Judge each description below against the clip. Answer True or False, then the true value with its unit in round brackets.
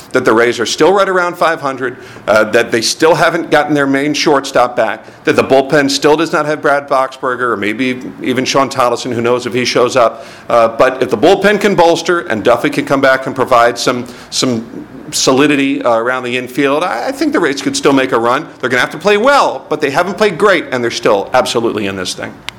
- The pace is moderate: False (235 wpm)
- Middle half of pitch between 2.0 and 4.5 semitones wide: False (5.0 semitones)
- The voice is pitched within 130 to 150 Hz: True (140 Hz)